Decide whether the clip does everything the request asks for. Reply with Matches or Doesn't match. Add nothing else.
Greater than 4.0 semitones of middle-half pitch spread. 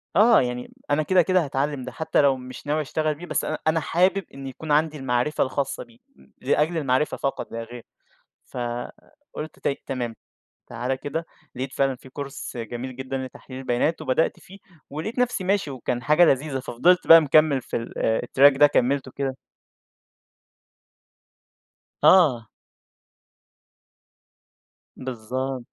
Doesn't match